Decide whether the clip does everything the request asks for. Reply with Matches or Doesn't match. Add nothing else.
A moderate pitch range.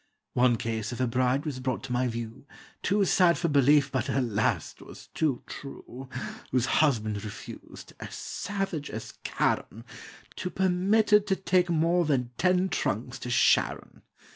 Doesn't match